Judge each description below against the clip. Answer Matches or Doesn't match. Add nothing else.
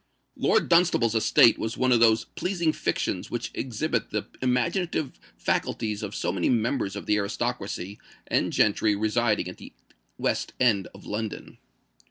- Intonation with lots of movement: Doesn't match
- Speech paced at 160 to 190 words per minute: Doesn't match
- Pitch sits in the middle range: Doesn't match